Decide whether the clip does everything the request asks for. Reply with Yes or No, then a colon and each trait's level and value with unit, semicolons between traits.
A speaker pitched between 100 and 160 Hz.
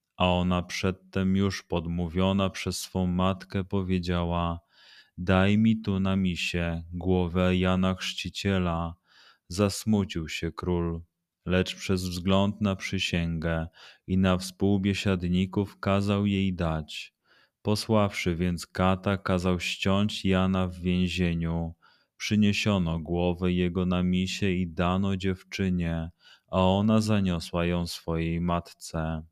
No: very low, 90 Hz